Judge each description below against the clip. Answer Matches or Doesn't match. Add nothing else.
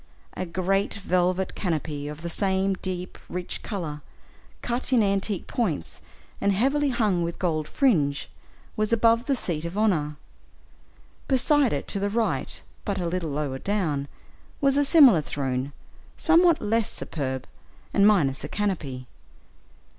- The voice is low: Doesn't match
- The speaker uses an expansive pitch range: Matches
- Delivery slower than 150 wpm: Matches